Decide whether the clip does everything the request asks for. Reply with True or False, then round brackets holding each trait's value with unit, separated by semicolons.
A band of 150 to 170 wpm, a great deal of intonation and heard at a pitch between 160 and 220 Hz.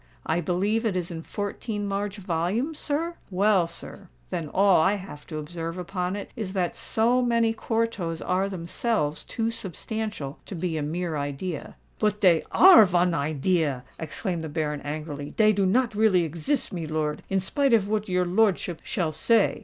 False (165 wpm; 4.7 semitones; 185 Hz)